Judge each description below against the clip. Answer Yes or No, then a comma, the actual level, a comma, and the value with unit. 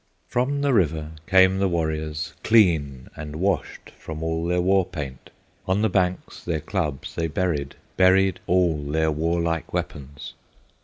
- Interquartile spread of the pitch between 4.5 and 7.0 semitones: No, average, 3.4 semitones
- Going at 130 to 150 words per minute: Yes, average, 145 wpm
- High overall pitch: No, very low, 85 Hz